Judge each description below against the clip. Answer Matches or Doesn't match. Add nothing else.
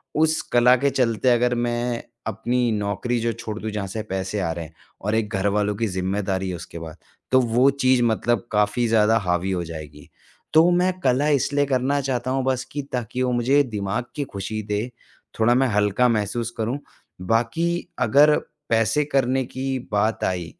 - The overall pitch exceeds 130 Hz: Doesn't match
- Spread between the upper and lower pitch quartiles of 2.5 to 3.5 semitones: Doesn't match